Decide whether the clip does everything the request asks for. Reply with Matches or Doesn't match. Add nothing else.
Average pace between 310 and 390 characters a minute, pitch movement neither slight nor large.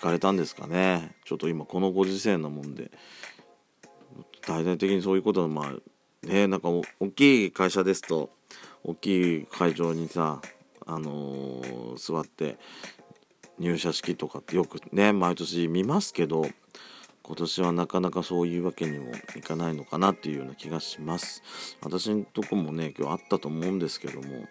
Matches